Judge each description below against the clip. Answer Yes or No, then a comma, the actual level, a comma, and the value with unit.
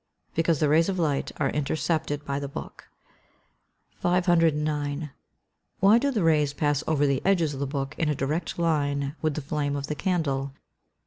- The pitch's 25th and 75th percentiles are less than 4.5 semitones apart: Yes, narrow, 2.6 semitones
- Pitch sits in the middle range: Yes, medium, 150 Hz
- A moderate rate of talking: Yes, average, 180 wpm